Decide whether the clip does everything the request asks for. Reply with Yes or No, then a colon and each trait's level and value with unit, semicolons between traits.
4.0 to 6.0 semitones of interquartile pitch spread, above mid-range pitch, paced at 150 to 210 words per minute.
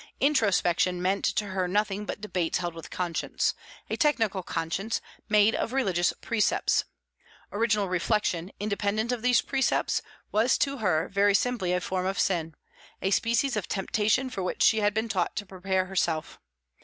No: average, 3.3 semitones; high, 200 Hz; average, 160 wpm